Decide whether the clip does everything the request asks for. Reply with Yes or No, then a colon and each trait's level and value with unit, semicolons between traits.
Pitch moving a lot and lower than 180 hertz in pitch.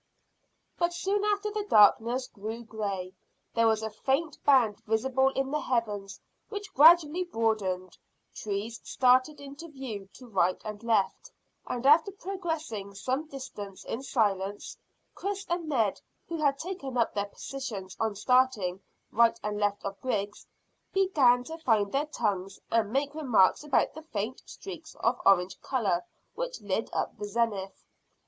No: wide, 6.6 semitones; high, 240 Hz